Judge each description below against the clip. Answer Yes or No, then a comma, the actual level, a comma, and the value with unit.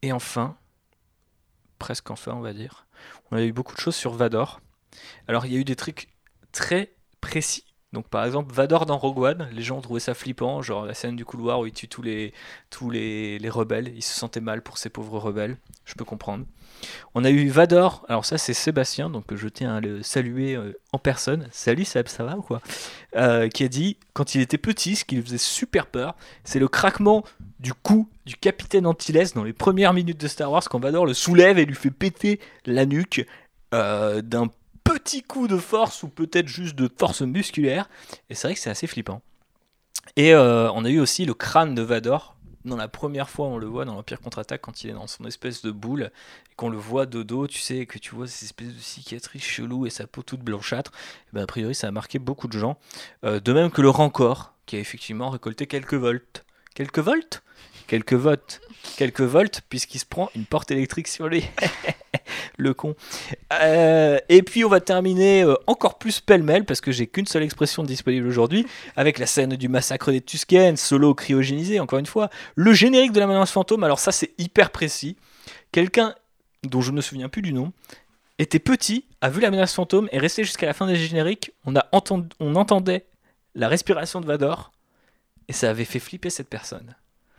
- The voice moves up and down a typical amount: No, wide, 6.1 semitones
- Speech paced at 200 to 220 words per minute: Yes, average, 210 wpm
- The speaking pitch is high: No, low, 135 Hz